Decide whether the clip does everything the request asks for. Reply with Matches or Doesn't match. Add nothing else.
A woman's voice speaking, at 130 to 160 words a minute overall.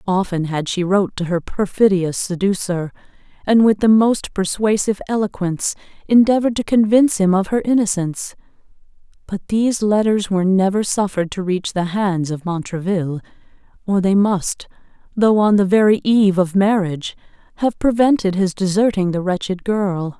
Matches